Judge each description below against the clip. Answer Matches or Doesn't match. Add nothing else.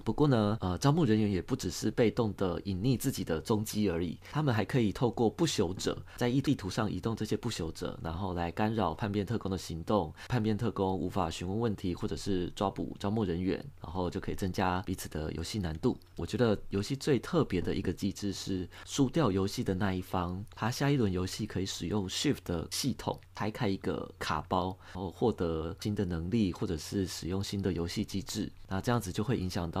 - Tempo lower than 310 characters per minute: Doesn't match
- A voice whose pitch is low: Matches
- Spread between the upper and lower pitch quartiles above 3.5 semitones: Doesn't match